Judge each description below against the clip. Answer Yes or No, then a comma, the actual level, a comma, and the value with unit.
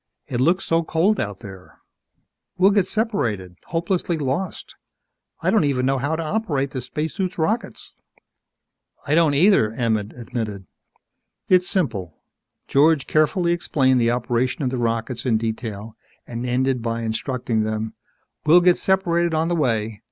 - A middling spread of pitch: No, wide, 6.7 semitones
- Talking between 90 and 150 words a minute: Yes, average, 145 wpm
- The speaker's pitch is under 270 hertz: Yes, low, 135 Hz